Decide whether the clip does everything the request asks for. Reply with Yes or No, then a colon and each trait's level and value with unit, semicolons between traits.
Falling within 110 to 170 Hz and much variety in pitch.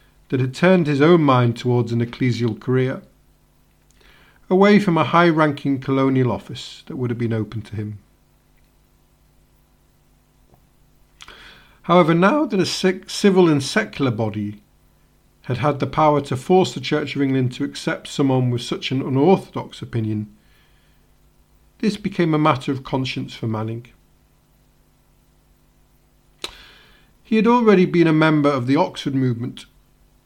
Yes: low, 135 Hz; wide, 6.1 semitones